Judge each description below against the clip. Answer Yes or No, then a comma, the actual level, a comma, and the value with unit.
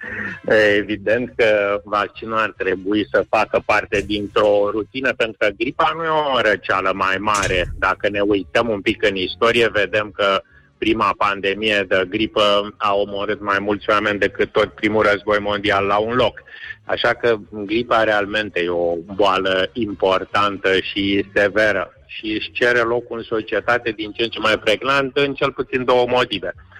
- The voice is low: Yes, low, 105 Hz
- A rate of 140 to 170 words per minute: Yes, average, 165 wpm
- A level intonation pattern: Yes, narrow, 2.2 semitones